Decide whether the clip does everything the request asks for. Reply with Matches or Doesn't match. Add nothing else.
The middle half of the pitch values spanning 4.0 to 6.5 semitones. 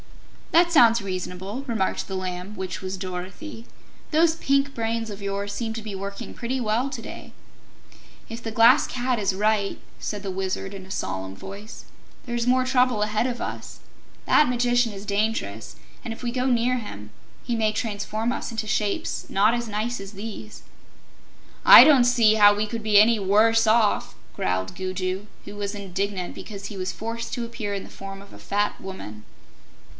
Doesn't match